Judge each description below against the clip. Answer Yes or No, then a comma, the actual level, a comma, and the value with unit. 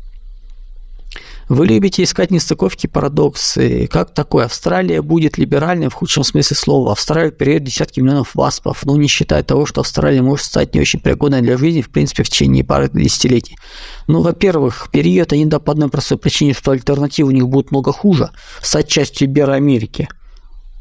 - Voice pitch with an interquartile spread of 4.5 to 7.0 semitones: No, average, 3.9 semitones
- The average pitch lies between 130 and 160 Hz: Yes, medium, 140 Hz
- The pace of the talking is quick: Yes, fast, 170 wpm